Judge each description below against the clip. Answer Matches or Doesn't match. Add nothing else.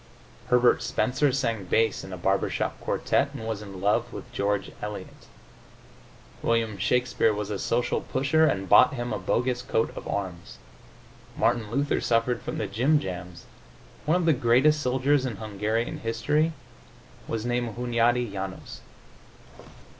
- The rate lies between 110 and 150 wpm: Matches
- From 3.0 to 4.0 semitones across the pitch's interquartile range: Matches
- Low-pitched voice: Matches